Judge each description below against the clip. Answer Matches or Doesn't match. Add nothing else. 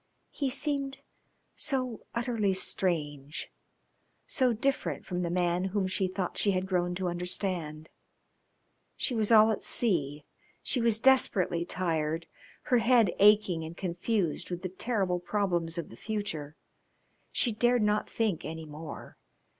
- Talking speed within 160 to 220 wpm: Doesn't match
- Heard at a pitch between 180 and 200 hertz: Matches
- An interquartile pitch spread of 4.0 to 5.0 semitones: Matches